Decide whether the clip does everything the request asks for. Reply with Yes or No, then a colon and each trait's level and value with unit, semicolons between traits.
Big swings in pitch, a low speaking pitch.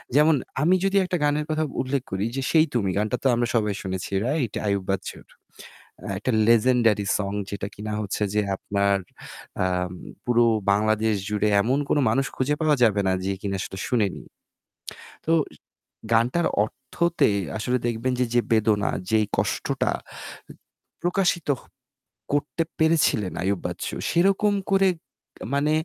Yes: wide, 6.3 semitones; low, 115 Hz